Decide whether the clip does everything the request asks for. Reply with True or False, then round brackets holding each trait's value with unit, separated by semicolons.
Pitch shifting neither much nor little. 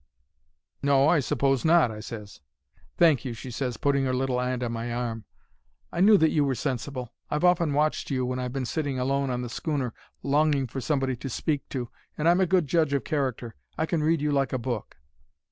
True (3.3 semitones)